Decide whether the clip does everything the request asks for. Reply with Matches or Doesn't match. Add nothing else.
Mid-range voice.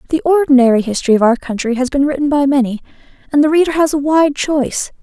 Doesn't match